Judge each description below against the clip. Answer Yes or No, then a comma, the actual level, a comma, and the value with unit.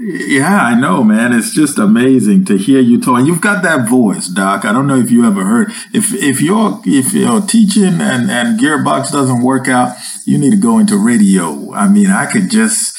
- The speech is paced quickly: Yes, fast, 215 wpm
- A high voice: Yes, high, 210 Hz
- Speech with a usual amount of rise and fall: No, wide, 5.8 semitones